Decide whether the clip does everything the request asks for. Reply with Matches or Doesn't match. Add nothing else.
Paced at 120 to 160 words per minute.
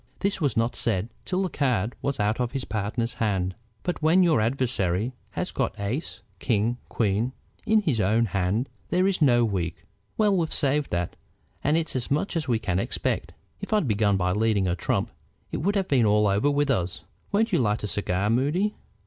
Doesn't match